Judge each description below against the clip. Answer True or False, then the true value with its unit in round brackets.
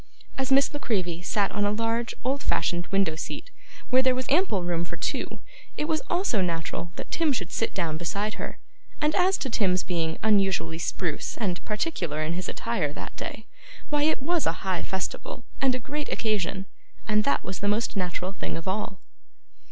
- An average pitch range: False (6.7 semitones)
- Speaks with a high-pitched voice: True (205 Hz)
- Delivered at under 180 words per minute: False (190 wpm)